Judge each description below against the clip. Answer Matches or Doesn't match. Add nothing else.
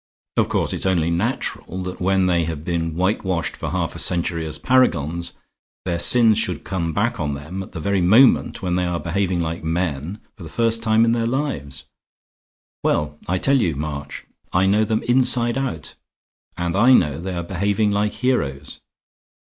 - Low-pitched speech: Matches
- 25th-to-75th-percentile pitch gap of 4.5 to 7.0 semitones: Matches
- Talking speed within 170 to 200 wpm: Matches